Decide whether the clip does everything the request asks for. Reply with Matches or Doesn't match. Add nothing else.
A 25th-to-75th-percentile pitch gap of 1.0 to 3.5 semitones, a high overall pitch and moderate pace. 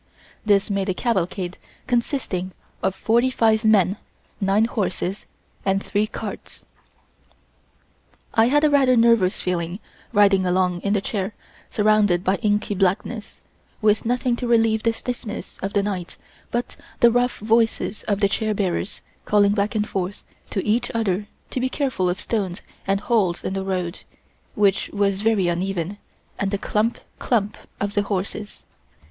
Matches